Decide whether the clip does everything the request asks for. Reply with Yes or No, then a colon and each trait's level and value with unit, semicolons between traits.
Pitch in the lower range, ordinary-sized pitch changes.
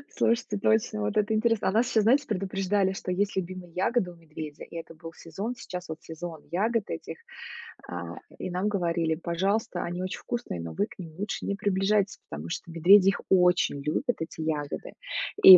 No: medium, 185 Hz; average, 3.9 semitones